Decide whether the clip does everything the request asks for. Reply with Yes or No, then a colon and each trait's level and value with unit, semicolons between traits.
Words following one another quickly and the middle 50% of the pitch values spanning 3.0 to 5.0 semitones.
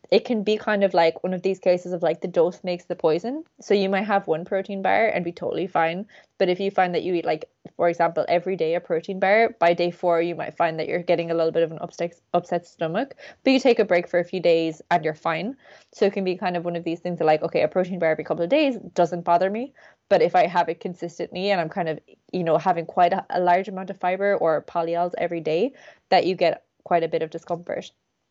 No: fast, 270 wpm; narrow, 2.5 semitones